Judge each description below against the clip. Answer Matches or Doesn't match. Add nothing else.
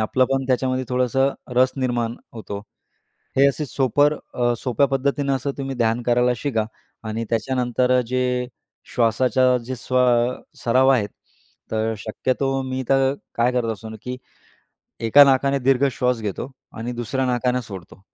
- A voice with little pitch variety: Matches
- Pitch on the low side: Matches